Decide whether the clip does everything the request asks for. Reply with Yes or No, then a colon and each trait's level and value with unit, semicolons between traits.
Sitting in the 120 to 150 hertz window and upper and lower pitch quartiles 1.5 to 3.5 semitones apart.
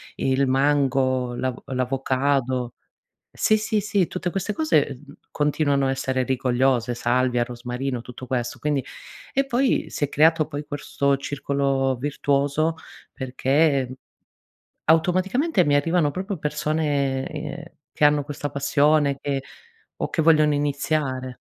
Yes: medium, 140 Hz; average, 2.7 semitones